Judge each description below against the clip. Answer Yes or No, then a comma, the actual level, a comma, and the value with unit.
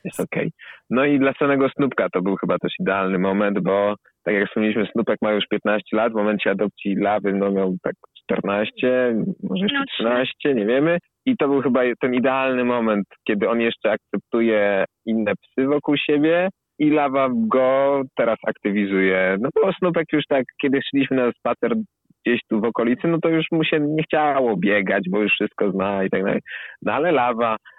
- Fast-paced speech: Yes, fast, 185 wpm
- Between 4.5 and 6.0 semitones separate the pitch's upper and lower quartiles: Yes, wide, 5.6 semitones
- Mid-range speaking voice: No, low, 120 Hz